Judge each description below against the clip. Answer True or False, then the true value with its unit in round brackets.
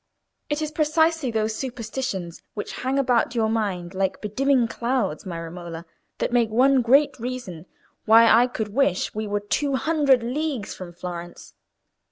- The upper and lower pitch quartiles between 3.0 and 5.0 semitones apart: False (5.4 semitones)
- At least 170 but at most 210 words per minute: False (155 wpm)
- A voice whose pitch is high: True (230 Hz)